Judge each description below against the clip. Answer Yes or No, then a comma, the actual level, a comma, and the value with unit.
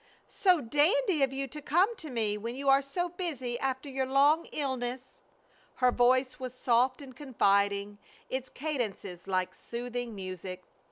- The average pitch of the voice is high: Yes, very high, 260 Hz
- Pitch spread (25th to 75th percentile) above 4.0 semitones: No, average, 3.4 semitones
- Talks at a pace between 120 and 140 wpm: No, average, 155 wpm